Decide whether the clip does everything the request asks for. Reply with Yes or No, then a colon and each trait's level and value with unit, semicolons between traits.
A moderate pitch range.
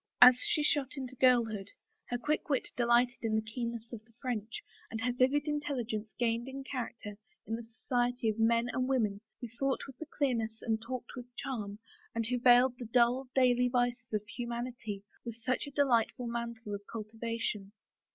No: narrow, 2.1 semitones